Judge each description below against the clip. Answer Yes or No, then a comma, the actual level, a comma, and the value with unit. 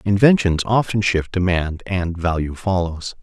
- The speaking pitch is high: No, very low, 95 Hz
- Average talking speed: No, slow, 130 wpm